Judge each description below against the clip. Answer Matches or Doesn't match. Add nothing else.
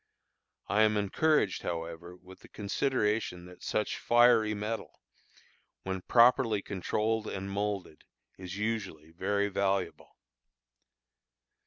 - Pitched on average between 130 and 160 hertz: Doesn't match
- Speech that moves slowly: Matches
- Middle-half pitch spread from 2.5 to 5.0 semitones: Matches